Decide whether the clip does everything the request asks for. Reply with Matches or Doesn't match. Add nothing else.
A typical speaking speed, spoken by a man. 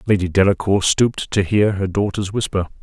Matches